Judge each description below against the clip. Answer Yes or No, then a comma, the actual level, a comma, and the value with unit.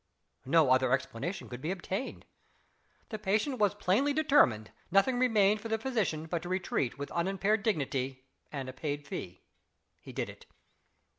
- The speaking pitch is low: No, medium, 185 Hz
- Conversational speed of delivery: Yes, average, 155 wpm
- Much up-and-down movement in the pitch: Yes, wide, 7.8 semitones